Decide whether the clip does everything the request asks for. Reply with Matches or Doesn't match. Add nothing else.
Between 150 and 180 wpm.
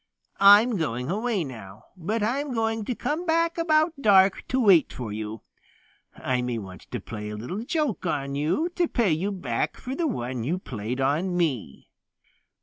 Matches